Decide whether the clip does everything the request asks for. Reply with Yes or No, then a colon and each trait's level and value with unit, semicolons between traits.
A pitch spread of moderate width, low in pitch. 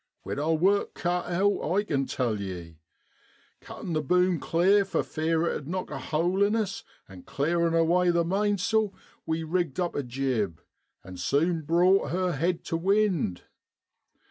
No: average, 4.5 semitones; medium, 170 Hz